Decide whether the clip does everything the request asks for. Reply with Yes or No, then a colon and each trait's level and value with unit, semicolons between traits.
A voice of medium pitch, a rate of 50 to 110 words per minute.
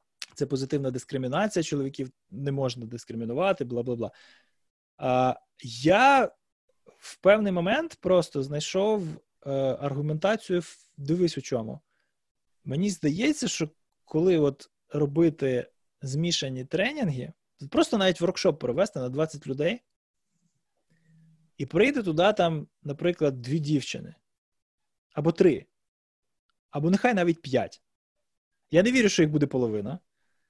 Yes: medium, 155 Hz; slow, 105 wpm